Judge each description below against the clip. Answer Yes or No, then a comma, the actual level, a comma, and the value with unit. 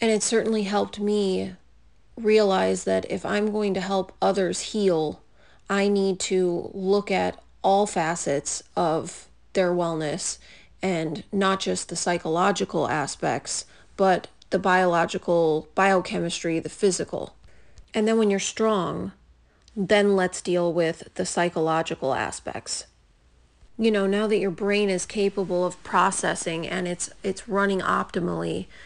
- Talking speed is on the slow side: Yes, slow, 130 wpm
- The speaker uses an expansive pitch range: No, average, 3.2 semitones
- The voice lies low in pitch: No, medium, 185 Hz